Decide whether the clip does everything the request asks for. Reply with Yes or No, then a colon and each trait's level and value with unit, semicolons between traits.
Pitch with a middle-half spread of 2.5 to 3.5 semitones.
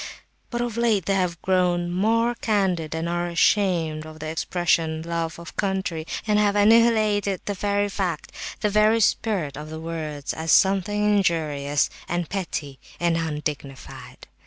No: average, 4.3 semitones